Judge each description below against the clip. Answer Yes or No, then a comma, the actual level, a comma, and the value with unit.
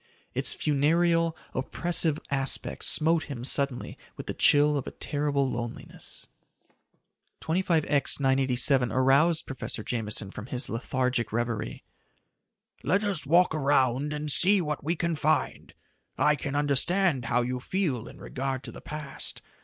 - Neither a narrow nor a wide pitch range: Yes, average, 3.8 semitones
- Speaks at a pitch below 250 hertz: Yes, medium, 140 Hz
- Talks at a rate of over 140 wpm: No, slow, 135 wpm